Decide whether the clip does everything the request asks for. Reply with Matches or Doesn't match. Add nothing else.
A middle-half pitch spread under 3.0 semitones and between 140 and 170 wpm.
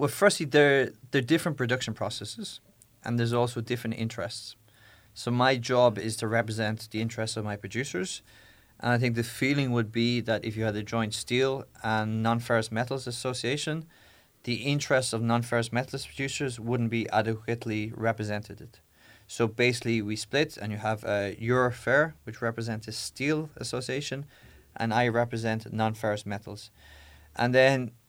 Matches